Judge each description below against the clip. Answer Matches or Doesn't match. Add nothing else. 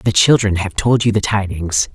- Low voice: Matches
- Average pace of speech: Doesn't match